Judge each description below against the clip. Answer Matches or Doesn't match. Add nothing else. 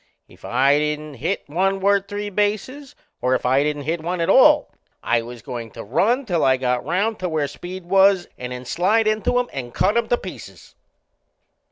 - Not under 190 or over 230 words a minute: Matches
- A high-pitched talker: Doesn't match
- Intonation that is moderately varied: Doesn't match